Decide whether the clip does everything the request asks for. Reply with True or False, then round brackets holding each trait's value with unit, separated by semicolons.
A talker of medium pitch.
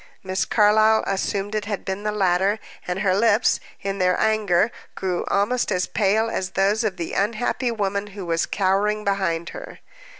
False (200 Hz)